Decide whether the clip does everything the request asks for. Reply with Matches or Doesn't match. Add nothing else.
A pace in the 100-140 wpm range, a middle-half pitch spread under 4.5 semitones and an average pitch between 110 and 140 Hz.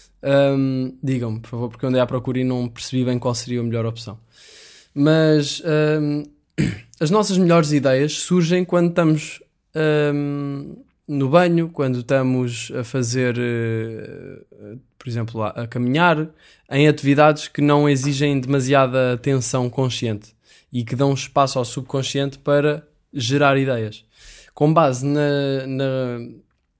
Matches